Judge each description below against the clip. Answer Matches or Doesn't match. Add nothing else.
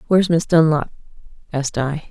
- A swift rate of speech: Doesn't match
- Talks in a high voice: Doesn't match